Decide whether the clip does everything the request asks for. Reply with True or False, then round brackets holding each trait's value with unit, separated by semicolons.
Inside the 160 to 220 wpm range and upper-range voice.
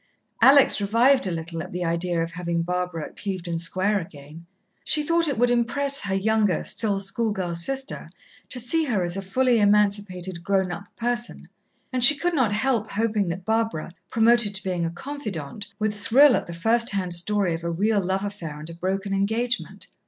True (190 wpm; 200 Hz)